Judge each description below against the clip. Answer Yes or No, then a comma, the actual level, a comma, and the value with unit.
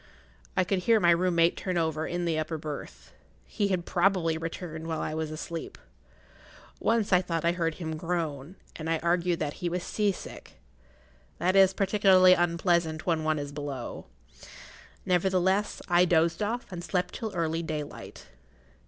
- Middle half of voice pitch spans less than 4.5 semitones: Yes, narrow, 2.4 semitones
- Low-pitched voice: No, medium, 170 Hz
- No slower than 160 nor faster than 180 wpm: Yes, average, 170 wpm